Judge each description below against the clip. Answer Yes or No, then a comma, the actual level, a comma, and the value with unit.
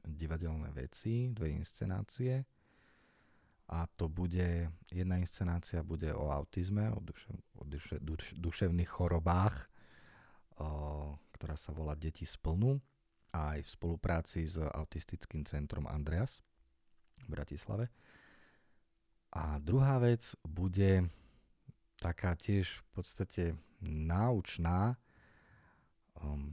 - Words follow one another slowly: Yes, slow, 95 wpm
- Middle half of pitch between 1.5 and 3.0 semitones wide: No, average, 3.9 semitones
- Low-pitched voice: Yes, very low, 85 Hz